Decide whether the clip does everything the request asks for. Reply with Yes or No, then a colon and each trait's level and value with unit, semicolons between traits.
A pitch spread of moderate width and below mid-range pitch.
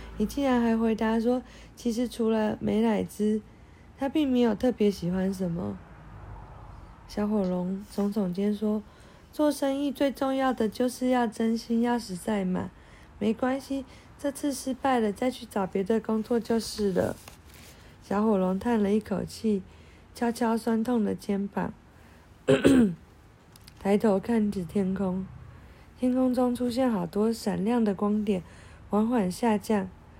No: average, 3.6 semitones; high, 215 Hz